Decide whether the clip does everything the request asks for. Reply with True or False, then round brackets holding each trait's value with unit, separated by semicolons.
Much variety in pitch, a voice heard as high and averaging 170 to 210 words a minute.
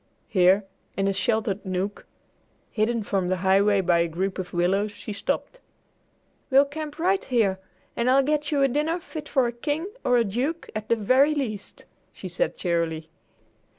True (6.6 semitones; 215 Hz; 175 wpm)